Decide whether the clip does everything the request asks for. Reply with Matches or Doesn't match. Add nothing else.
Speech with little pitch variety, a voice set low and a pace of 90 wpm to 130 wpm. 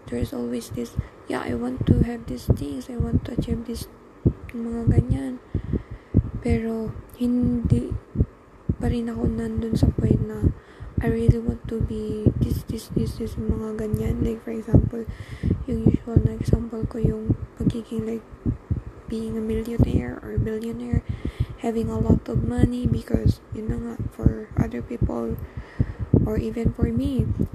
Doesn't match